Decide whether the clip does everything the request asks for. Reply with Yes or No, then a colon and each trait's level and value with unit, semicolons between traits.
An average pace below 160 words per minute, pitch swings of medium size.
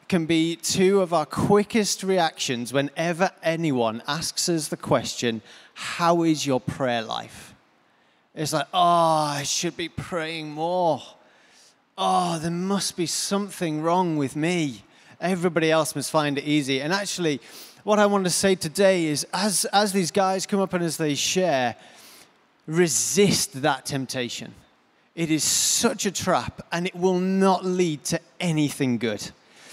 Yes: average, 150 wpm; average, 4.1 semitones